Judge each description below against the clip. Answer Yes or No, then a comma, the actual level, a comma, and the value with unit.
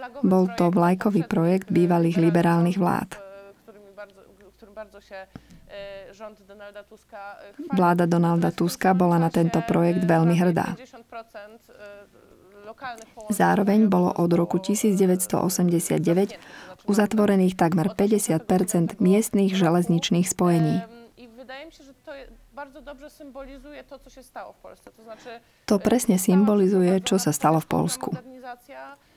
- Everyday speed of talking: No, slow, 70 wpm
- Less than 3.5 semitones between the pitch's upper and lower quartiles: No, average, 4.0 semitones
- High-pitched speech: Yes, high, 200 Hz